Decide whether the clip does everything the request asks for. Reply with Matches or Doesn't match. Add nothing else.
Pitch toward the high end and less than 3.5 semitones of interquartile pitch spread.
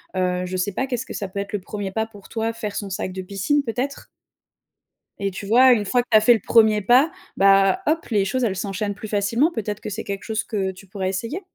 Matches